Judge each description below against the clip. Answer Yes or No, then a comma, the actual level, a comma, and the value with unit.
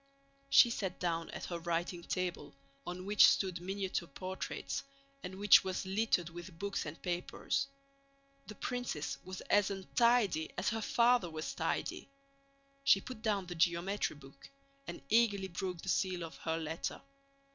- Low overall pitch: No, medium, 185 Hz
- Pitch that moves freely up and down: No, average, 3.2 semitones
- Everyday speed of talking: Yes, average, 150 wpm